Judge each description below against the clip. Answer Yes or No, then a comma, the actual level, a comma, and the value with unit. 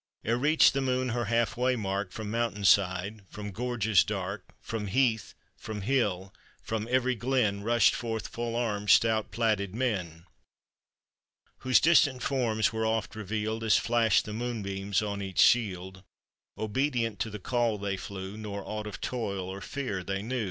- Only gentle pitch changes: No, average, 3.2 semitones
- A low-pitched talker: Yes, low, 110 Hz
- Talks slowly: No, average, 160 wpm